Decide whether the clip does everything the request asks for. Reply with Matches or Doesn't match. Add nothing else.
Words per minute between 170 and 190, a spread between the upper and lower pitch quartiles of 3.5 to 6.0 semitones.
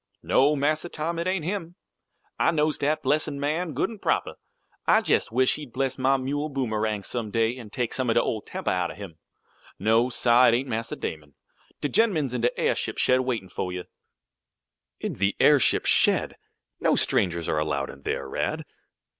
Matches